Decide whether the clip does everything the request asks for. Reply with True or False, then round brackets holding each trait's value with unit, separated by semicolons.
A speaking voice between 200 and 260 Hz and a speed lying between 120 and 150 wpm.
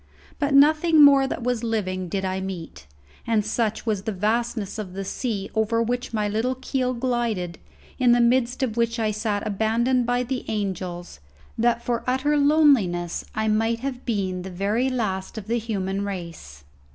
False (225 Hz; 175 wpm)